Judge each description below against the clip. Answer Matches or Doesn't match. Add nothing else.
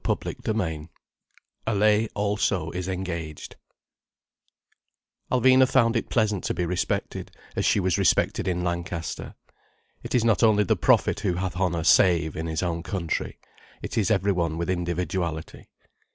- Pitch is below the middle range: Matches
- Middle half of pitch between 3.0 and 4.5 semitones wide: Matches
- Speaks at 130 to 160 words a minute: Matches